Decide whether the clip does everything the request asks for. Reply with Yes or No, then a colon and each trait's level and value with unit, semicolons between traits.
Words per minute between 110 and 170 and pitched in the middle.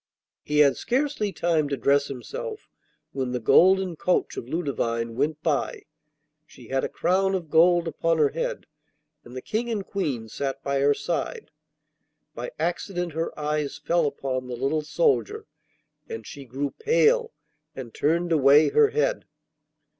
Yes: average, 155 wpm; medium, 155 Hz